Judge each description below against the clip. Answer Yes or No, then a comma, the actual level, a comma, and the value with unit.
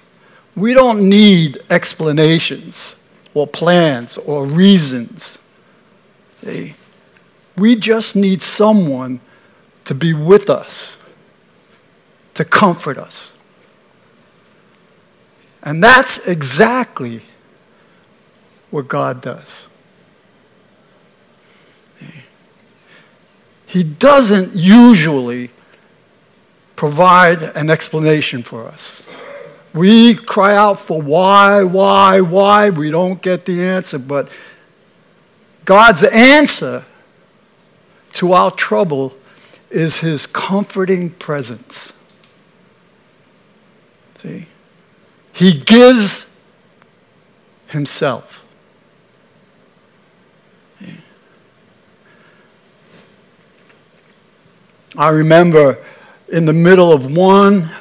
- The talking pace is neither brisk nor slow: No, slow, 70 wpm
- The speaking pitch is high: Yes, high, 195 Hz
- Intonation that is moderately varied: Yes, average, 4.4 semitones